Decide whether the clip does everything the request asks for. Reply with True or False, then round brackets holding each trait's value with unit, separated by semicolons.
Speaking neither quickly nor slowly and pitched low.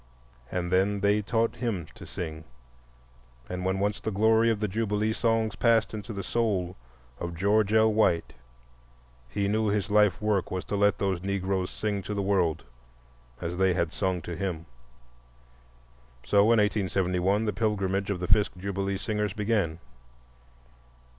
True (155 wpm; 100 Hz)